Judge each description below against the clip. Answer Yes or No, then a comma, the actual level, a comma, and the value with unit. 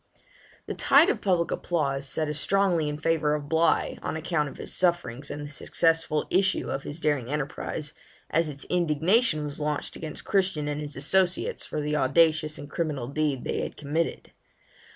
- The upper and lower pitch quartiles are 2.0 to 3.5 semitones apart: Yes, narrow, 2.5 semitones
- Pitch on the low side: No, medium, 155 Hz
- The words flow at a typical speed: Yes, average, 175 wpm